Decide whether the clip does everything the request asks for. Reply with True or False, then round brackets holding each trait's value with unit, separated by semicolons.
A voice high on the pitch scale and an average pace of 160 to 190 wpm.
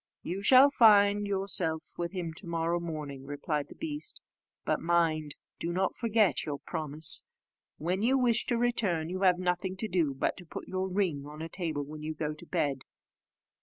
False (175 Hz; 185 wpm)